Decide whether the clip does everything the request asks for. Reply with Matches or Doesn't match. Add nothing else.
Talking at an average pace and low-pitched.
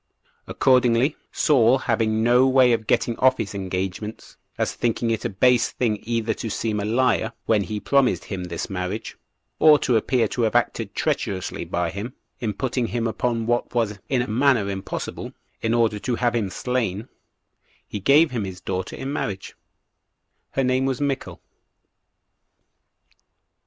Matches